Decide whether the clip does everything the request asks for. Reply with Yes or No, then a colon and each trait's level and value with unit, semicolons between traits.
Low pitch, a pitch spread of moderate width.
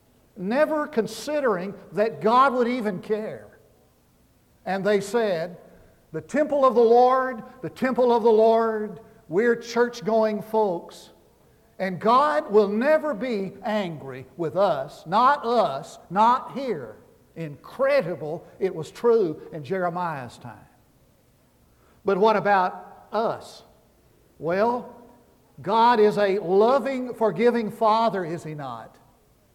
No: high, 220 Hz; average, 4.3 semitones